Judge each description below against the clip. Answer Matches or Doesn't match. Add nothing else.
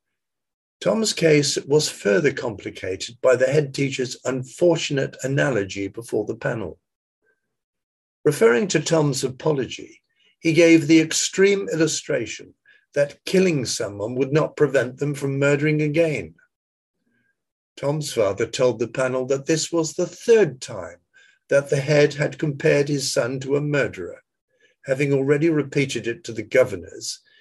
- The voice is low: Doesn't match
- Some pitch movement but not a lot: Matches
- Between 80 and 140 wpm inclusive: Matches